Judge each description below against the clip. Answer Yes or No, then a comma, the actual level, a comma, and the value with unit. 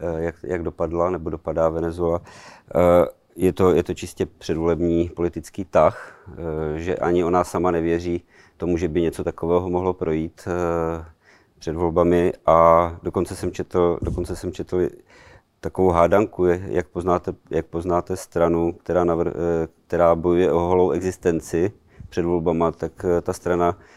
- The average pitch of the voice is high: No, very low, 85 Hz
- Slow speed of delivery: No, average, 135 wpm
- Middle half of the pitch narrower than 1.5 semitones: Yes, narrow, 1.1 semitones